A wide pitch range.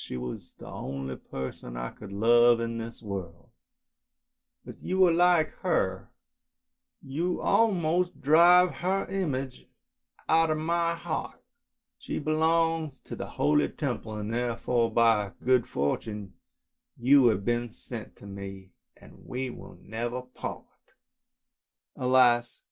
Yes: wide, 7.5 semitones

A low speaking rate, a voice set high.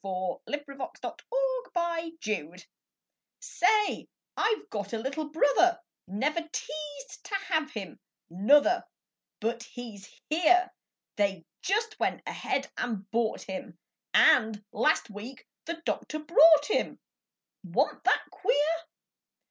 Yes: slow, 110 wpm; very high, 290 Hz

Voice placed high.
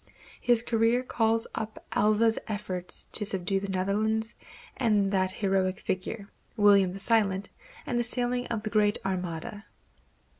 Yes: high, 210 Hz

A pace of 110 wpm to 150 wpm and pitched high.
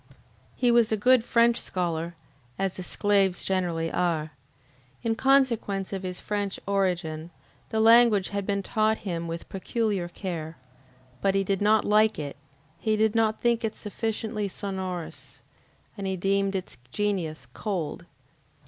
Yes: average, 145 wpm; high, 200 Hz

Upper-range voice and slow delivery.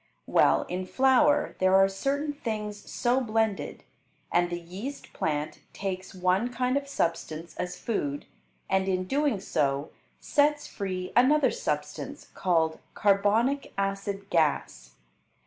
Yes: high, 195 Hz; slow, 125 wpm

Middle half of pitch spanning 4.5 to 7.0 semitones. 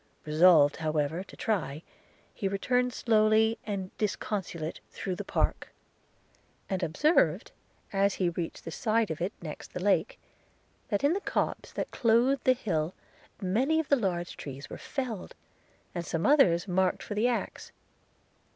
Yes: average, 5.1 semitones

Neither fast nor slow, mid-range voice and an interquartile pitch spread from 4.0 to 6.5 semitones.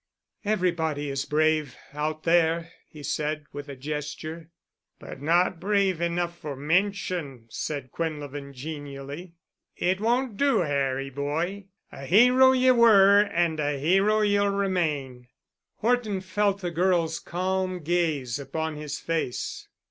No: slow, 125 wpm; medium, 165 Hz; average, 4.8 semitones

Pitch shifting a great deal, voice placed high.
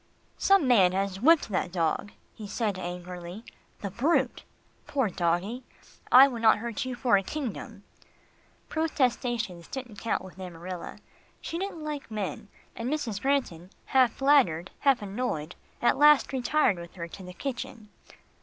Yes: wide, 6.3 semitones; high, 225 Hz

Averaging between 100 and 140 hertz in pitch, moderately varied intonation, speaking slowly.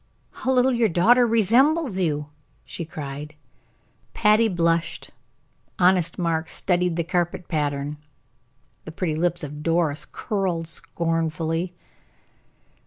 No: medium, 170 Hz; average, 3.2 semitones; slow, 105 wpm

